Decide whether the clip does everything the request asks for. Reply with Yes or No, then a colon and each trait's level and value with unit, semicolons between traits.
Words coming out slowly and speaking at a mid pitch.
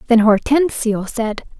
No: slow, 115 wpm; high, 235 Hz